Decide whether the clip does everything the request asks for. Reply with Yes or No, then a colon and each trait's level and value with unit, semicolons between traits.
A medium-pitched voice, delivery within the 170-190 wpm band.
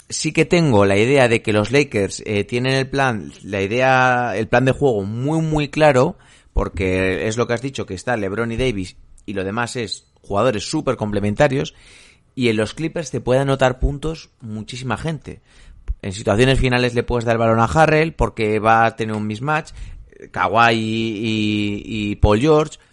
No: low, 115 Hz; average, 185 wpm